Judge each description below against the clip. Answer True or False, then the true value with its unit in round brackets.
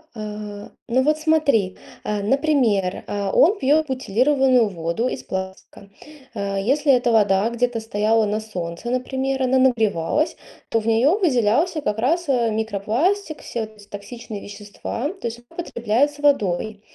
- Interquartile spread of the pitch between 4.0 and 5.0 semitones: True (4.6 semitones)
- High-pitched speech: True (230 Hz)